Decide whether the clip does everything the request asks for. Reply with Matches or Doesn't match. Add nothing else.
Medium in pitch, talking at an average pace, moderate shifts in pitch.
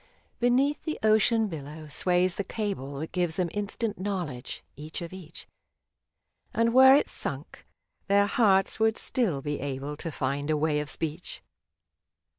Doesn't match